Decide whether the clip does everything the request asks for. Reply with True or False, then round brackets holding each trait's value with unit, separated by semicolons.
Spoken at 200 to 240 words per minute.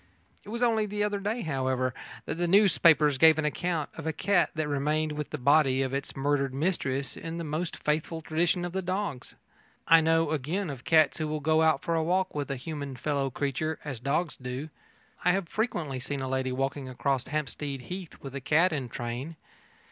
True (205 wpm)